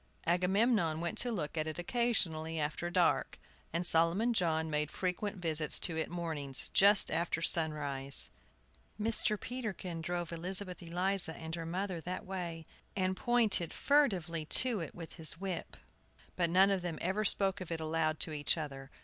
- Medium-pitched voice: Yes, medium, 175 Hz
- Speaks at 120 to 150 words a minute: No, average, 160 wpm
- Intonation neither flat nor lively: Yes, average, 3.2 semitones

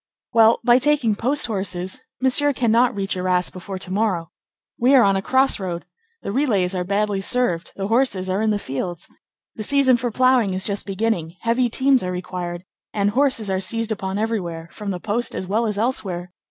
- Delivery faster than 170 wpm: Yes, average, 190 wpm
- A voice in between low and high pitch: No, high, 205 Hz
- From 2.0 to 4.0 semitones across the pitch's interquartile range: No, average, 4.4 semitones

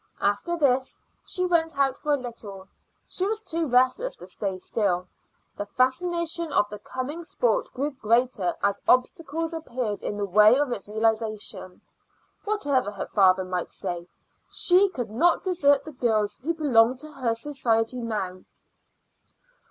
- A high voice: Yes, very high, 255 Hz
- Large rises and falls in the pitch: Yes, wide, 7.4 semitones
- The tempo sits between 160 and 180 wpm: No, average, 150 wpm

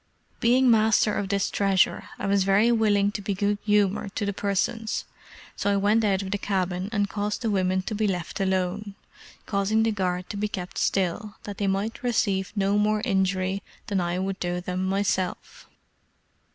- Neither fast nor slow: Yes, average, 185 wpm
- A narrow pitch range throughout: Yes, narrow, 1.8 semitones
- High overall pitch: Yes, high, 200 Hz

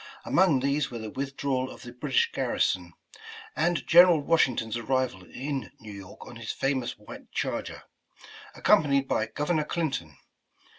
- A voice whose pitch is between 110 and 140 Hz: Yes, low, 135 Hz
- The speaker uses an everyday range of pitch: Yes, average, 4.3 semitones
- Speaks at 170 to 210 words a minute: No, average, 145 wpm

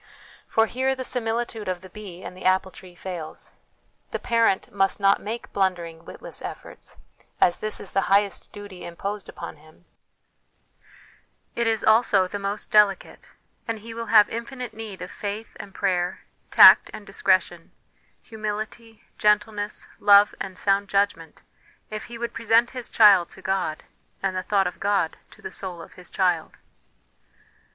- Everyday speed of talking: Yes, average, 160 wpm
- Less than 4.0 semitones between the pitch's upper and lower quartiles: Yes, average, 3.0 semitones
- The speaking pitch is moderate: No, high, 200 Hz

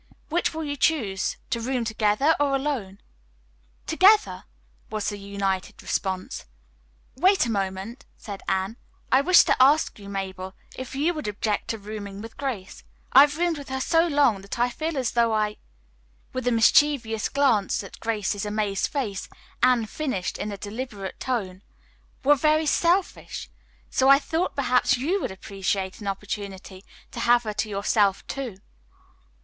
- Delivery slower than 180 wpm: Yes, average, 160 wpm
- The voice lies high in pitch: Yes, high, 230 Hz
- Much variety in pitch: Yes, wide, 5.9 semitones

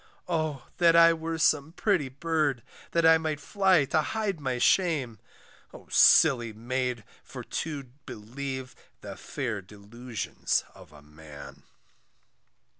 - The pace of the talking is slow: Yes, slow, 125 wpm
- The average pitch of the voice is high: No, medium, 140 Hz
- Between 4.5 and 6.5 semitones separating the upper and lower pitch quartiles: Yes, wide, 5.4 semitones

